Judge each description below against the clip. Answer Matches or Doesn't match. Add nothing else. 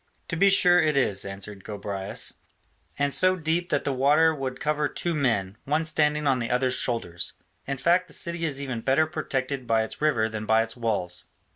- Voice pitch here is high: Doesn't match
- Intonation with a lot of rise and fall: Matches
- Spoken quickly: Doesn't match